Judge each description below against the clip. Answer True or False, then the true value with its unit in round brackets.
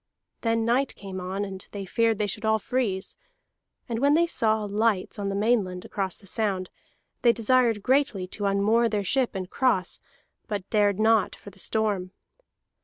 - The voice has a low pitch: False (210 Hz)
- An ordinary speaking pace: True (175 wpm)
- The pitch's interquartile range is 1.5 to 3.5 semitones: True (2.7 semitones)